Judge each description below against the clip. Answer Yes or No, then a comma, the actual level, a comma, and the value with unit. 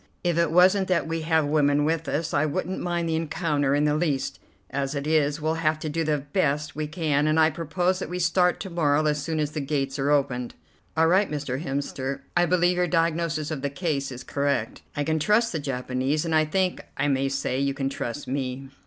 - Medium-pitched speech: Yes, medium, 150 Hz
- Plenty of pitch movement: No, average, 2.9 semitones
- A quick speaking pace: Yes, fast, 225 wpm